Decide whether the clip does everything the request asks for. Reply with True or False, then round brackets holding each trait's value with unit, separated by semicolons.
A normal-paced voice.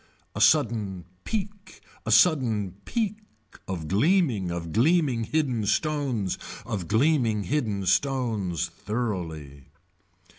False (100 wpm)